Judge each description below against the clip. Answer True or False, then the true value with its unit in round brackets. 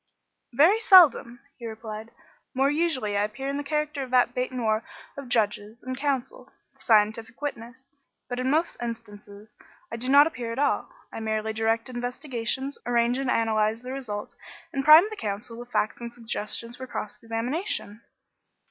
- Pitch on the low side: False (240 Hz)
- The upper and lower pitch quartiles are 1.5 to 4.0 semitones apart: True (3.6 semitones)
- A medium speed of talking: True (165 wpm)